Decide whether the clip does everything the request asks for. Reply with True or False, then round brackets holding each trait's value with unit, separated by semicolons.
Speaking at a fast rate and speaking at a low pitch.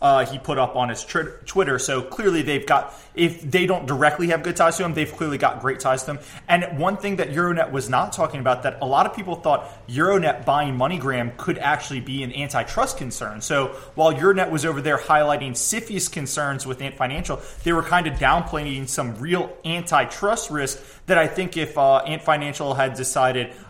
False (210 wpm; 145 Hz)